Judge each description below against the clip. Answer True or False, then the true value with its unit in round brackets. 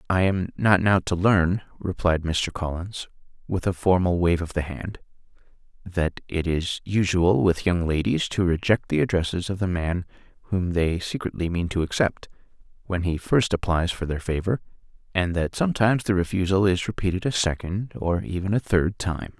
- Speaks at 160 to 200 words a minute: True (175 wpm)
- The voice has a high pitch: False (90 Hz)